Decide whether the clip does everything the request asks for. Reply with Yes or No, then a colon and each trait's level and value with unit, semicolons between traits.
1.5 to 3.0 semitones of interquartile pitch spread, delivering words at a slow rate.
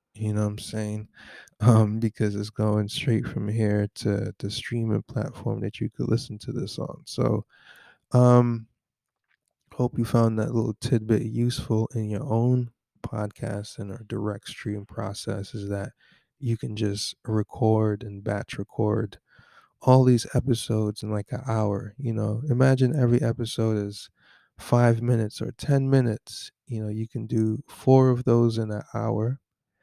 No: narrow, 2.4 semitones; average, 160 wpm